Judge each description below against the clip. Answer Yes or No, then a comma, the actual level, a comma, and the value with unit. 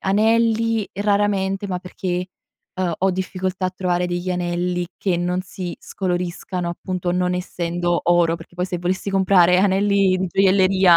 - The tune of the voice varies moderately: No, narrow, 1.5 semitones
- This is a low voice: No, medium, 185 Hz